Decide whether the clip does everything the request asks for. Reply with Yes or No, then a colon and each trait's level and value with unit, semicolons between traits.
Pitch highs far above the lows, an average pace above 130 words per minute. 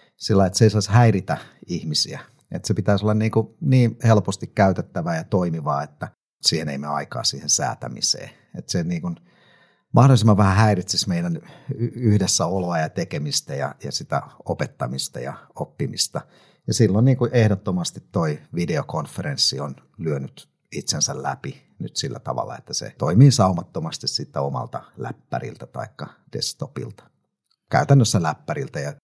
Yes: wide, 6.5 semitones; average, 140 wpm